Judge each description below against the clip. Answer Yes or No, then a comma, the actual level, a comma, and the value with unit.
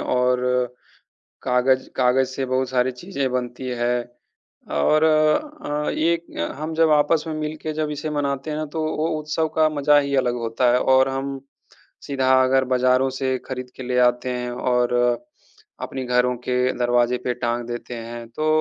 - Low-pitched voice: Yes, low, 130 Hz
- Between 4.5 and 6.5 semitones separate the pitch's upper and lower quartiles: No, average, 3.4 semitones